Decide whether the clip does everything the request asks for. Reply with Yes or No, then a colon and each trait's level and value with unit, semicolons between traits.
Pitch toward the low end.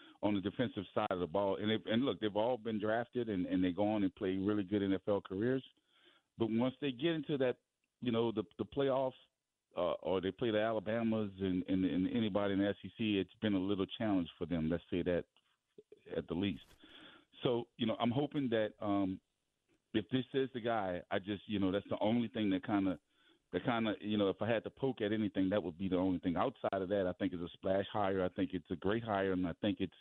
Yes: low, 105 Hz